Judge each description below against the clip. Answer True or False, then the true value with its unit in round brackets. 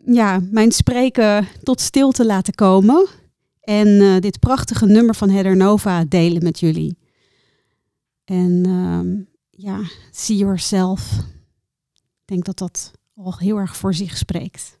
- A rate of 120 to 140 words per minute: True (135 wpm)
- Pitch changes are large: False (3.6 semitones)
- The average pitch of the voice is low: False (190 Hz)